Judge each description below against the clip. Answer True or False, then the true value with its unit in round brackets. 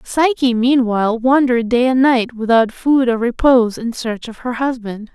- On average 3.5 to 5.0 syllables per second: True (4.8 syllables/s)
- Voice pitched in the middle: False (240 Hz)